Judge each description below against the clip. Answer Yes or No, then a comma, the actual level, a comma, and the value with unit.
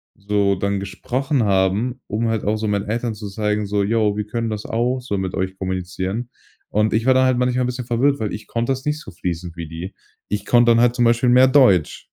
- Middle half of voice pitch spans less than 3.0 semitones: No, average, 3.6 semitones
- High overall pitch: No, low, 110 Hz